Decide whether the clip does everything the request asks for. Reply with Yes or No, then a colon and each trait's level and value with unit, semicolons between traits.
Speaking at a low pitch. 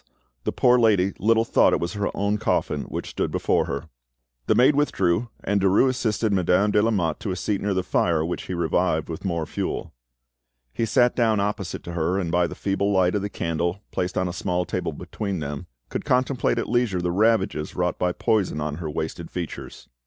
Yes: very low, 95 Hz